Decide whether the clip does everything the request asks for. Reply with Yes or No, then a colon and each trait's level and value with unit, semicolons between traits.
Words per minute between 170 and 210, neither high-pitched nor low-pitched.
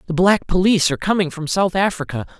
Yes: average, 200 wpm; medium, 175 Hz